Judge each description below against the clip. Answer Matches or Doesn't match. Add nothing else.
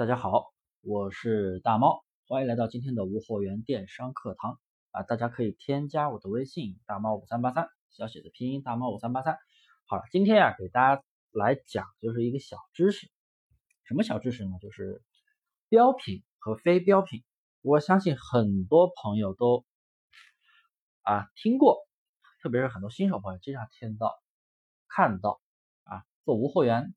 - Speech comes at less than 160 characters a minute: Doesn't match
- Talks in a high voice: Doesn't match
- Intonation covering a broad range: Matches